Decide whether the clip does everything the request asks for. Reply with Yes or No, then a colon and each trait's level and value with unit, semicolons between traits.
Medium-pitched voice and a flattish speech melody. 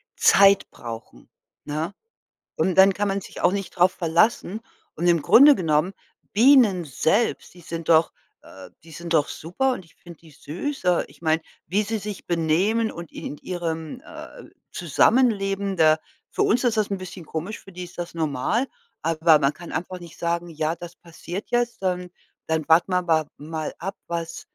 No: medium, 175 Hz; average, 3.5 semitones